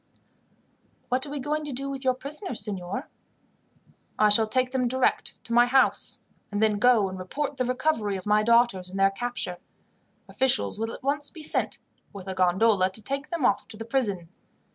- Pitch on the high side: Yes, high, 235 Hz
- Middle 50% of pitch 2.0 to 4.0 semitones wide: No, average, 4.9 semitones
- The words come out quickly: No, average, 190 wpm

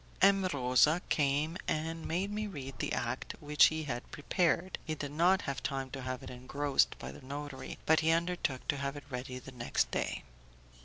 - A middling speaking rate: Yes, average, 195 wpm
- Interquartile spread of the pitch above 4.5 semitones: No, average, 3.7 semitones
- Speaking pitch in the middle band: Yes, medium, 145 Hz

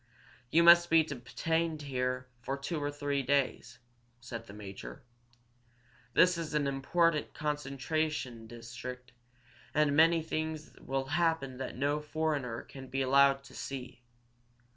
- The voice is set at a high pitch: No, medium, 140 Hz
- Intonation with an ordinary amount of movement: Yes, average, 3.6 semitones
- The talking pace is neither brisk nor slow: No, slow, 130 wpm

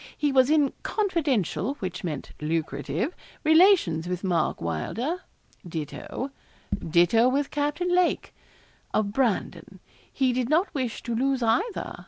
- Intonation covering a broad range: Yes, wide, 8.8 semitones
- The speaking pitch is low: No, very high, 250 Hz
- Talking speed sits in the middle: No, slow, 125 wpm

